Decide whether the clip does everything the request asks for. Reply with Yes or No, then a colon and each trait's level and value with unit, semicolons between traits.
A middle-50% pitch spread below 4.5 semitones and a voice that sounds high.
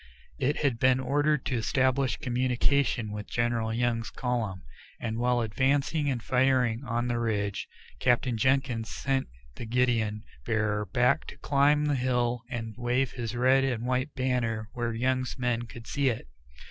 No: narrow, 2.4 semitones; low, 125 Hz